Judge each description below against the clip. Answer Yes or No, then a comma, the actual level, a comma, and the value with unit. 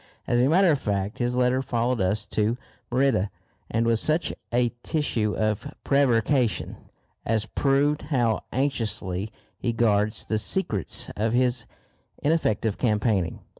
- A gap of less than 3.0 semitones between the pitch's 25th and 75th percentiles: No, average, 3.9 semitones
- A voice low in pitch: Yes, low, 120 Hz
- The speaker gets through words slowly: Yes, slow, 130 wpm